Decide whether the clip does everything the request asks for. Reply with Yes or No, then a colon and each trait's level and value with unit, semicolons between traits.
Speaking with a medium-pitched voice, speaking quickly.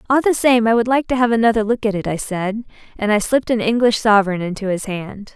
No: high, 220 Hz; fast, 260 wpm